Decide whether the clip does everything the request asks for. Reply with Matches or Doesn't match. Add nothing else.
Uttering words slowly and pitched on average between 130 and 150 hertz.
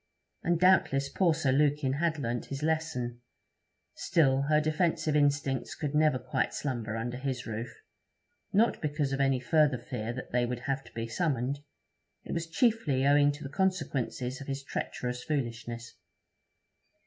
Doesn't match